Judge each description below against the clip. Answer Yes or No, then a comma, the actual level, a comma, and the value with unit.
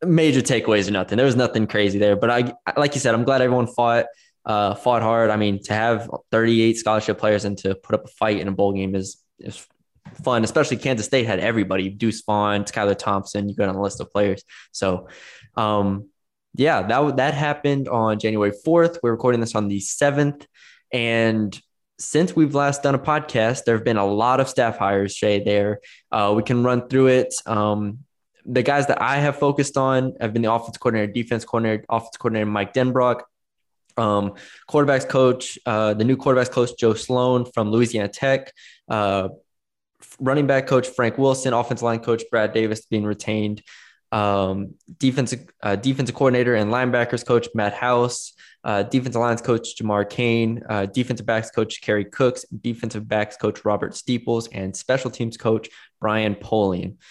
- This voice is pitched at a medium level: No, low, 115 Hz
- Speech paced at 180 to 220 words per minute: Yes, average, 185 wpm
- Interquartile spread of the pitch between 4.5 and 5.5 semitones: No, average, 3.6 semitones